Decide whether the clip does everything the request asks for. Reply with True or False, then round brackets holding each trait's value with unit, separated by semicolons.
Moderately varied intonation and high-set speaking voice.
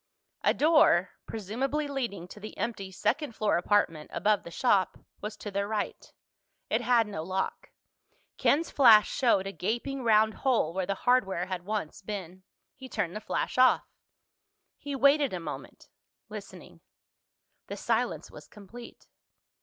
True (4.9 semitones; 215 Hz)